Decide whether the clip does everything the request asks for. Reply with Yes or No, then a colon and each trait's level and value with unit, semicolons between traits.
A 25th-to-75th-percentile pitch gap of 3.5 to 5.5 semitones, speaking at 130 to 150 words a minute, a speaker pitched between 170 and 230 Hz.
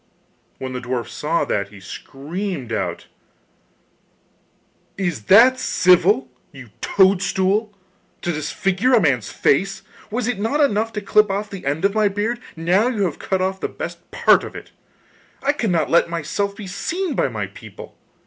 No: average, 4.8 semitones; average, 160 wpm; high, 190 Hz